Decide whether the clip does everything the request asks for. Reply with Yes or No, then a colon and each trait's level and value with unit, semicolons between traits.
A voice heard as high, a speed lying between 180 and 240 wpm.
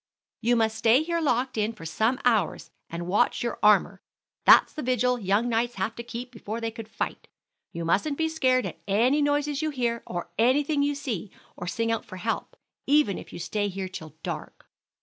Yes: high, 235 Hz; average, 200 wpm